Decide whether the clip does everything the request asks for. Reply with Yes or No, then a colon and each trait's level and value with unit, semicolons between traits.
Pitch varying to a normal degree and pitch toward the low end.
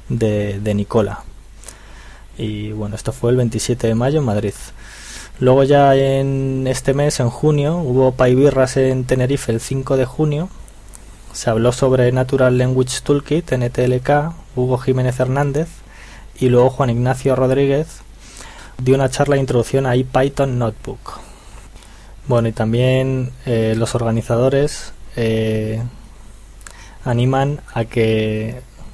Yes: average, 3.1 semitones; low, 125 Hz